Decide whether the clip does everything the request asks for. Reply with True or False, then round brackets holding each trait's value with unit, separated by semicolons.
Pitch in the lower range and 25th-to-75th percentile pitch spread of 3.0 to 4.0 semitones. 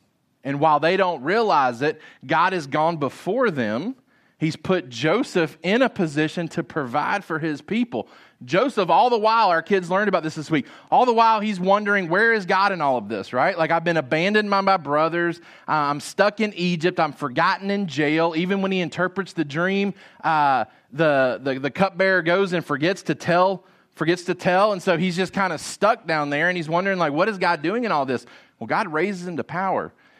False (175 Hz; 3.7 semitones)